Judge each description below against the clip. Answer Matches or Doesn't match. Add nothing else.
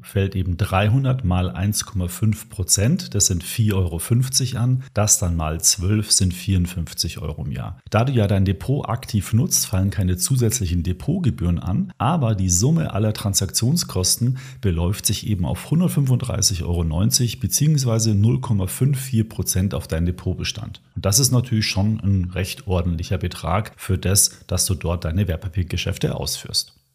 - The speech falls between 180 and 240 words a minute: Doesn't match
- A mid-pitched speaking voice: Doesn't match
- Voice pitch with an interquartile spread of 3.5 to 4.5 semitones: Matches